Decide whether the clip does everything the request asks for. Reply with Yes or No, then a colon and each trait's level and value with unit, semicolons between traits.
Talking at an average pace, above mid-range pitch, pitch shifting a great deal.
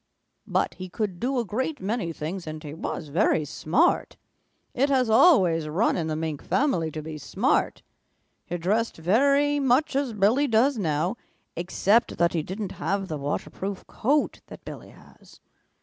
Yes: average, 165 wpm; high, 195 Hz; wide, 7.5 semitones